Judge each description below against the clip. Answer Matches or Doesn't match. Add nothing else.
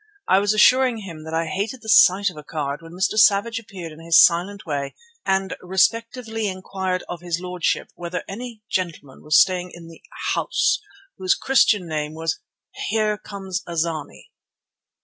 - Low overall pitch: Doesn't match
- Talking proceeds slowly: Doesn't match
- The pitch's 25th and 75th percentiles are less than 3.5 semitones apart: Doesn't match